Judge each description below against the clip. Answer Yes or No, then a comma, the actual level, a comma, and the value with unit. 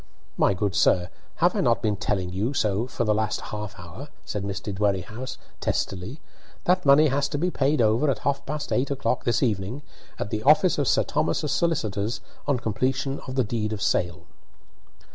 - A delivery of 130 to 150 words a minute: No, average, 185 wpm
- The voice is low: Yes, low, 115 Hz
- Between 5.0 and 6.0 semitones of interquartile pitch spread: Yes, wide, 5.4 semitones